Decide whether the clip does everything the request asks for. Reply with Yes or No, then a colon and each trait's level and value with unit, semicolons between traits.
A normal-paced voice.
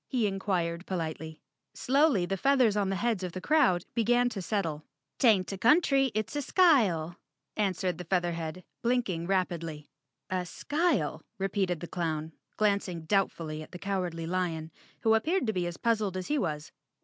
Yes: average, 165 wpm